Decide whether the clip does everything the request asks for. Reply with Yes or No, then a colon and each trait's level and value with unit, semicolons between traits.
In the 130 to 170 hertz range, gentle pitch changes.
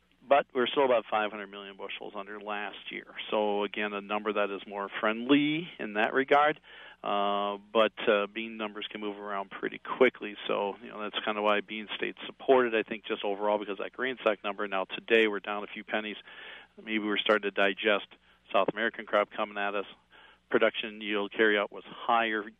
No: low, 105 Hz; narrow, 1.4 semitones